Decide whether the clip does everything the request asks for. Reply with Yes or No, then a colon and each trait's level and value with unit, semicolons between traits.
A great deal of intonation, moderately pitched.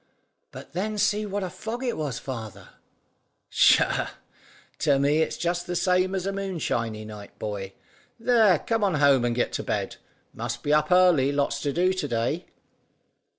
Yes: wide, 7.4 semitones; medium, 160 Hz